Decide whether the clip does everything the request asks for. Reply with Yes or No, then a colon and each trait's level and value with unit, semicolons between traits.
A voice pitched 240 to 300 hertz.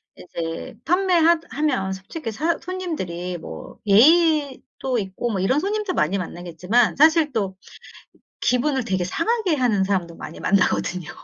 Yes: high, 245 Hz